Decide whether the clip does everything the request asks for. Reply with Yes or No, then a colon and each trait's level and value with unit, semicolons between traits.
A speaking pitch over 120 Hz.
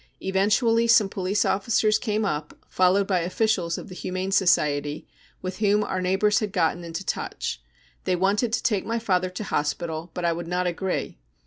Yes: high, 190 Hz